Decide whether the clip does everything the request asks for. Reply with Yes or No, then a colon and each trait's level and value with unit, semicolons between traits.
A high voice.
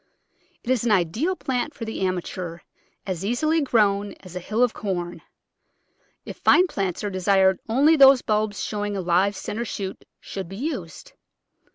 Yes: high, 205 Hz